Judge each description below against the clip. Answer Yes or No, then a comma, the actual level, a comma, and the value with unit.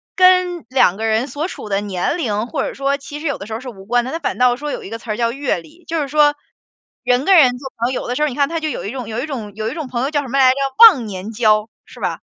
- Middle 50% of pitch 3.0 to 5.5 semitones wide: Yes, average, 4.7 semitones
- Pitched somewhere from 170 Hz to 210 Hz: No, very high, 255 Hz